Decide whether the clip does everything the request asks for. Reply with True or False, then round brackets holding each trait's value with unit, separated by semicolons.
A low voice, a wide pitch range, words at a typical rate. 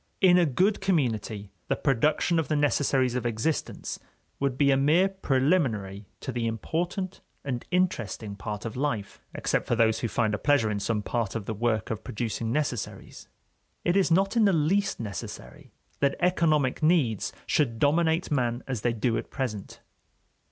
True (130 Hz; 6.3 semitones; 170 wpm)